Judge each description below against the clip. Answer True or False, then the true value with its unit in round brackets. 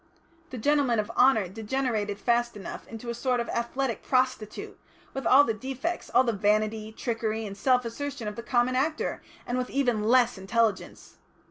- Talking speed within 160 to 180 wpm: True (170 wpm)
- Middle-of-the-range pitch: False (235 Hz)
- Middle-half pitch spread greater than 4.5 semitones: False (3.0 semitones)